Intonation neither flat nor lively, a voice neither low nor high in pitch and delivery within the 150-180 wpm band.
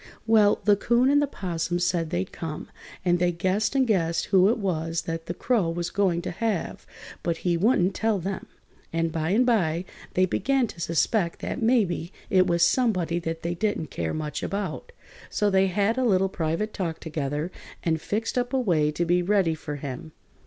No: average, 4.2 semitones; medium, 180 Hz; average, 195 wpm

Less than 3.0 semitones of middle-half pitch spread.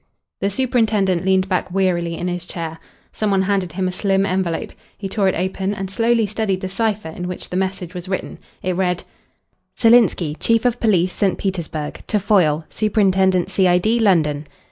Yes: narrow, 2.4 semitones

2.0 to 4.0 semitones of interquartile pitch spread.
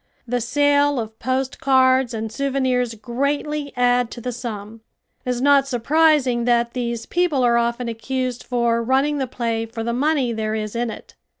Yes: narrow, 2.6 semitones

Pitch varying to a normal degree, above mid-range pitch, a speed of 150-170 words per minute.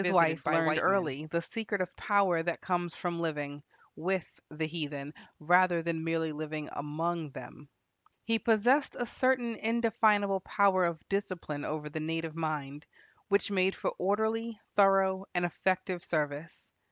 No: average, 4.2 semitones; medium, 175 Hz; average, 155 wpm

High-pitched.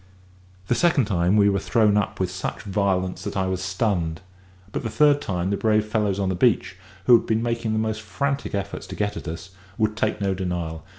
No: low, 100 Hz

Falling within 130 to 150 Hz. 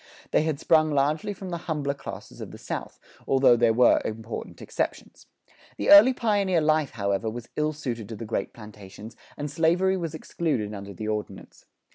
Yes: medium, 140 Hz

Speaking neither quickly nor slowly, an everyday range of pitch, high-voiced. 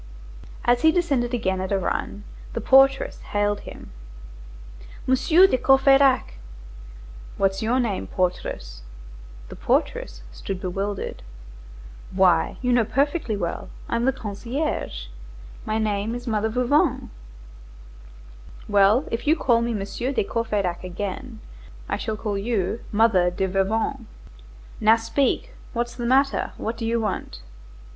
No: slow, 130 wpm; average, 4.3 semitones; high, 225 Hz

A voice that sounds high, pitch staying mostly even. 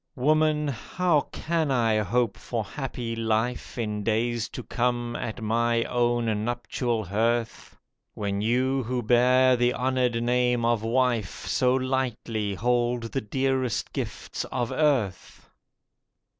No: low, 120 Hz; narrow, 2.1 semitones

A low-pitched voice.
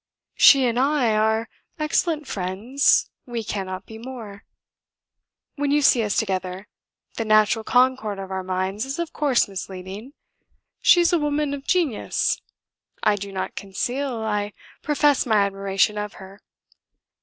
No: high, 220 Hz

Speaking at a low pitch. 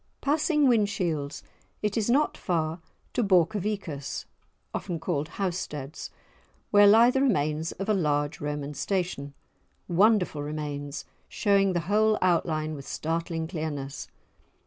No: medium, 170 Hz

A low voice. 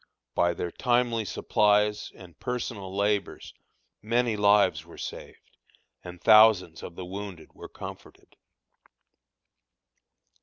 Yes: low, 105 Hz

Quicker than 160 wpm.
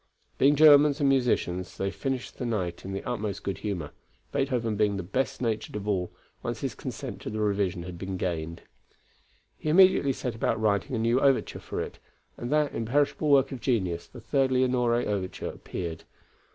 Yes: average, 180 wpm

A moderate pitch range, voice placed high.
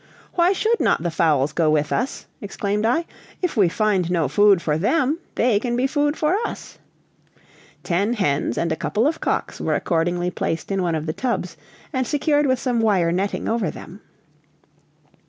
No: wide, 7.5 semitones; high, 205 Hz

